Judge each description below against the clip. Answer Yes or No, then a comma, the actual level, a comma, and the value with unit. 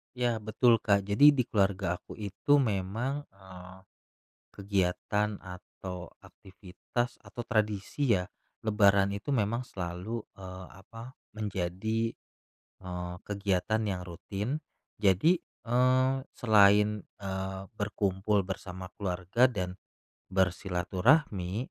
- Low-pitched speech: Yes, low, 100 Hz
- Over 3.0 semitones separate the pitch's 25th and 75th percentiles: Yes, average, 3.5 semitones